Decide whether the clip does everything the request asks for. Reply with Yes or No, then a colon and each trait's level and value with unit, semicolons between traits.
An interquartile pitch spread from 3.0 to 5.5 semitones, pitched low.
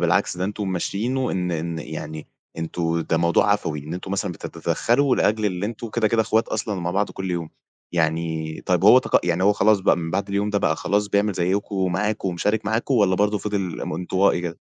Yes: average, 3.5 semitones; very low, 95 Hz